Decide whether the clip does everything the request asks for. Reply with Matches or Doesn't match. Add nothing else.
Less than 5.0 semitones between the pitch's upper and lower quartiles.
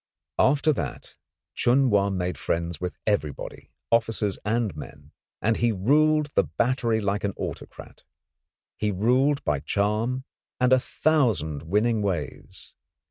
Doesn't match